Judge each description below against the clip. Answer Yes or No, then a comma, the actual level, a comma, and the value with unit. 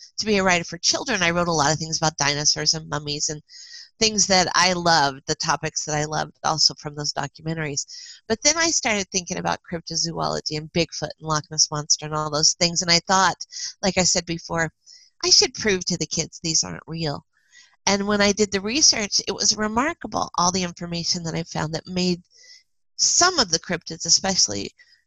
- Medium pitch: Yes, medium, 175 Hz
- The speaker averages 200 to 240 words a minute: Yes, fast, 205 wpm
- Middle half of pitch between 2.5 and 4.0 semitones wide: No, wide, 5.4 semitones